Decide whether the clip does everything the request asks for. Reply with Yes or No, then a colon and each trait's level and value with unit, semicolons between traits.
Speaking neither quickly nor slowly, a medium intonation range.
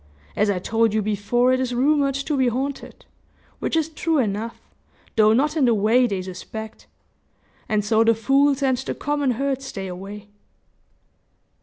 Yes: average, 165 wpm; average, 4.4 semitones